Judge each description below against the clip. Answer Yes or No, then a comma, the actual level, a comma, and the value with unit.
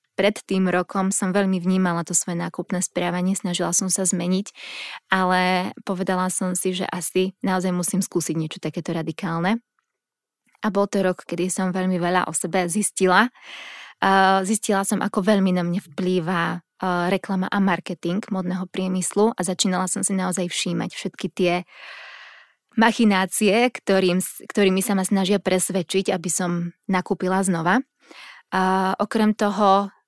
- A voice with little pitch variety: Yes, narrow, 1.7 semitones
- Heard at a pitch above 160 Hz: Yes, medium, 185 Hz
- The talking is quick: No, average, 140 wpm